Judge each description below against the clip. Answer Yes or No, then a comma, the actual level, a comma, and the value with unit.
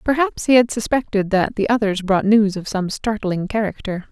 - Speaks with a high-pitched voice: Yes, high, 210 Hz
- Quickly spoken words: No, average, 190 wpm